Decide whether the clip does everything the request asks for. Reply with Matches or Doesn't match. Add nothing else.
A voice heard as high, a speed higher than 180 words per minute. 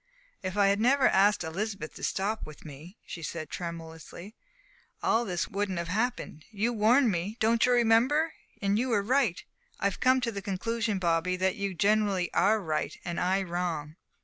Doesn't match